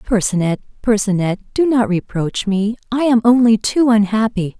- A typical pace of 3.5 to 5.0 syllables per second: Yes, 4.8 syllables/s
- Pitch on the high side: Yes, high, 220 Hz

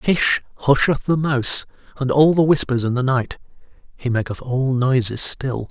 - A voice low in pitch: Yes, low, 130 Hz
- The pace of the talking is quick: No, average, 170 wpm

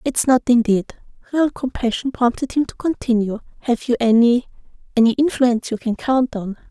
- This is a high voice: Yes, high, 245 Hz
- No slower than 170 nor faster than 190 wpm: No, average, 150 wpm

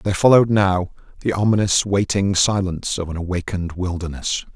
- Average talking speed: Yes, average, 145 wpm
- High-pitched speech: No, very low, 95 Hz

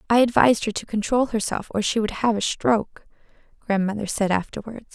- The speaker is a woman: Yes, female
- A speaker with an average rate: Yes, average, 180 wpm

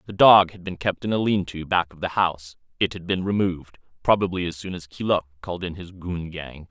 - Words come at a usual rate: No, fast, 240 wpm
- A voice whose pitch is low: Yes, very low, 90 Hz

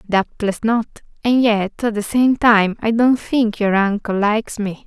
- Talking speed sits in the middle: Yes, average, 185 wpm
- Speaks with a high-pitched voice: Yes, high, 220 Hz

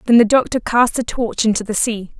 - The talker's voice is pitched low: No, high, 230 Hz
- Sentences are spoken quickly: Yes, fast, 245 wpm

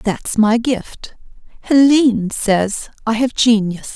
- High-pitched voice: Yes, high, 225 Hz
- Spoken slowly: Yes, slow, 120 wpm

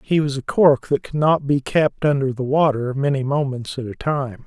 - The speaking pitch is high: No, medium, 140 Hz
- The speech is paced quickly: Yes, fast, 230 wpm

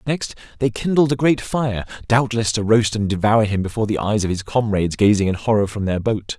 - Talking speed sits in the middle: No, fast, 215 wpm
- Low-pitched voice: Yes, low, 110 Hz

